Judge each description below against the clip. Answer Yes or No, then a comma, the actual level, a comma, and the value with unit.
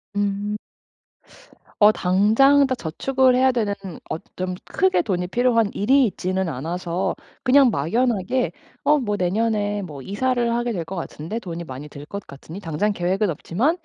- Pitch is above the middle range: Yes, high, 205 Hz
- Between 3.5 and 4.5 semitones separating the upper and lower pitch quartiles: No, average, 5.2 semitones